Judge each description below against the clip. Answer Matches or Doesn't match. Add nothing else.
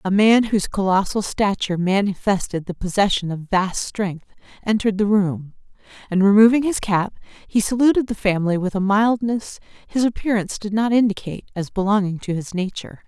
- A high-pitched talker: Matches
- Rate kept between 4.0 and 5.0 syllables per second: Doesn't match